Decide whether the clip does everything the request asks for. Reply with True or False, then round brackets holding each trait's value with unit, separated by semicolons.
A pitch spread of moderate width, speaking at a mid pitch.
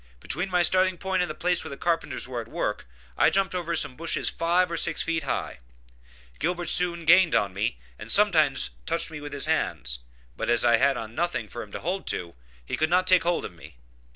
False (6.9 semitones; 165 Hz)